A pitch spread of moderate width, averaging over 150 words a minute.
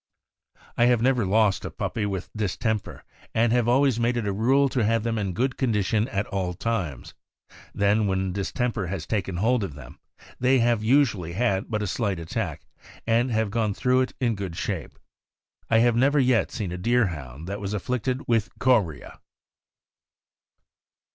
Yes: average, 3.9 semitones; average, 175 wpm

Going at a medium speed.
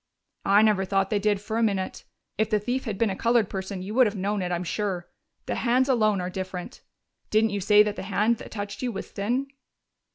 No: fast, 230 wpm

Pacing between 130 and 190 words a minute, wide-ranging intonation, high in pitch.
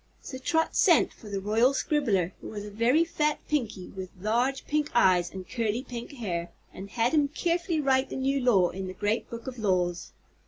No: average, 200 wpm; wide, 6.0 semitones; high, 235 Hz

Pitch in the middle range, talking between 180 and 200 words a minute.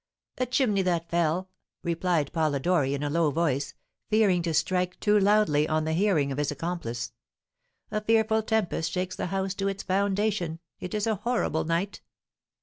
No: medium, 180 Hz; average, 165 wpm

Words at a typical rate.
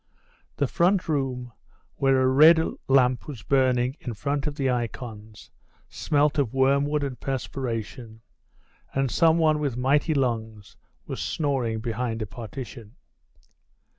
No: slow, 130 wpm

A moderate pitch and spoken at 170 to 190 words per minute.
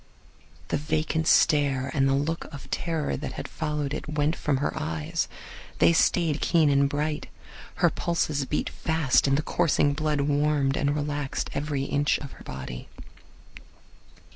No: medium, 145 Hz; average, 155 wpm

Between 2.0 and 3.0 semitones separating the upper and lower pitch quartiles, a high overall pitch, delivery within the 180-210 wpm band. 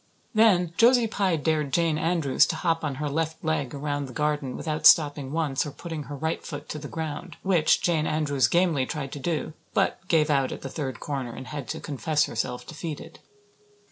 No: narrow, 2.6 semitones; medium, 150 Hz; average, 200 wpm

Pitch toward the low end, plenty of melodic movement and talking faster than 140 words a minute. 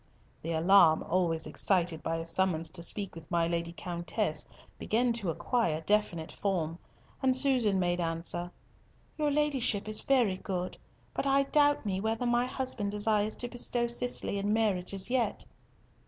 No: high, 200 Hz; wide, 5.9 semitones; average, 155 wpm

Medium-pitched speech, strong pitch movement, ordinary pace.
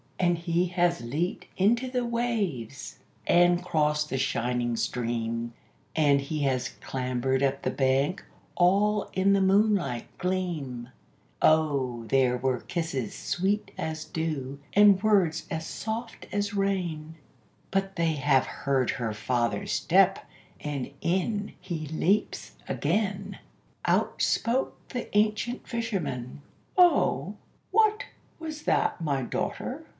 No: medium, 165 Hz; wide, 6.9 semitones; slow, 120 wpm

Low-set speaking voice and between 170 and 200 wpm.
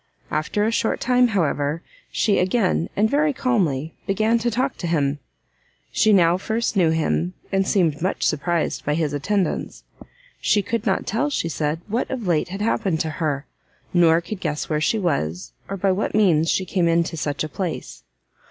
No: medium, 180 Hz; average, 180 wpm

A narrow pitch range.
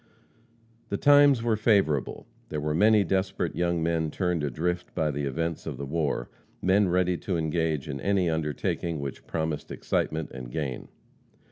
No: average, 3.7 semitones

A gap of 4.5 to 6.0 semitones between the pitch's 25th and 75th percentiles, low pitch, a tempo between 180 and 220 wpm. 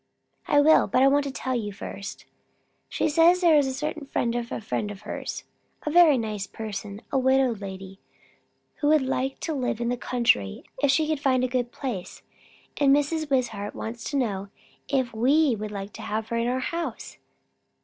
No: average, 4.8 semitones; very high, 255 Hz; average, 200 wpm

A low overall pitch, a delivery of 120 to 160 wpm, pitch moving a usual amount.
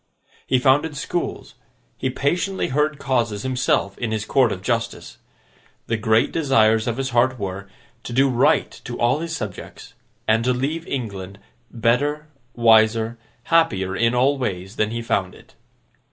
Yes: low, 120 Hz; average, 155 wpm; average, 3.7 semitones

